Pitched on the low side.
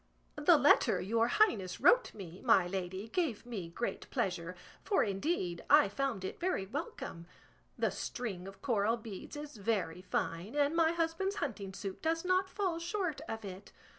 No: high, 225 Hz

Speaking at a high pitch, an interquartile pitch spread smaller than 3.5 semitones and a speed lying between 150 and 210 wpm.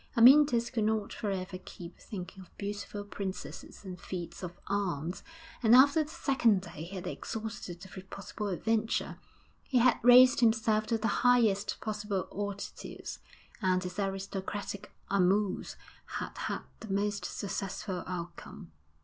No: high, 200 Hz; average, 3.0 semitones; average, 140 wpm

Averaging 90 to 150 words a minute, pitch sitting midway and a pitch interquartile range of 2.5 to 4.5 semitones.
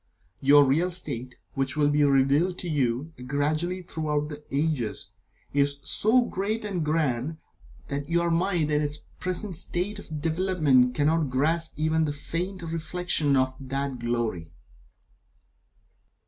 Yes: slow, 135 wpm; medium, 150 Hz; average, 3.7 semitones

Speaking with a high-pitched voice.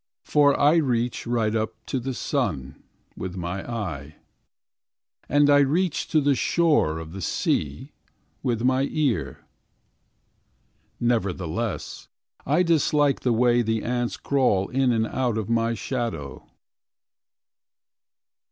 No: low, 120 Hz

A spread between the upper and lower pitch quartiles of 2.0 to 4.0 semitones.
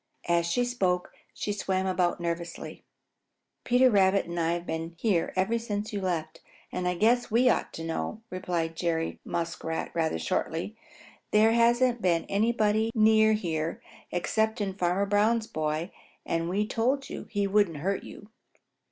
No: average, 4.4 semitones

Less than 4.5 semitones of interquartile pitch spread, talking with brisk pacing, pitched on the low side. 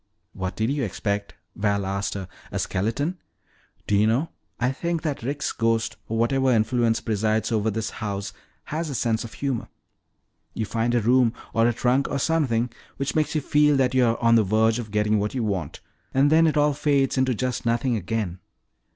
No: average, 3.9 semitones; average, 195 wpm; low, 115 Hz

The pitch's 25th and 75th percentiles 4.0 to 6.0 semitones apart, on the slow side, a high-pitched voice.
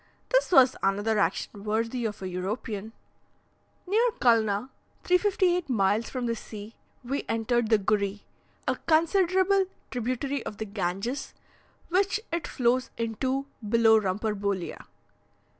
Yes: average, 5.1 semitones; slow, 120 wpm; high, 230 Hz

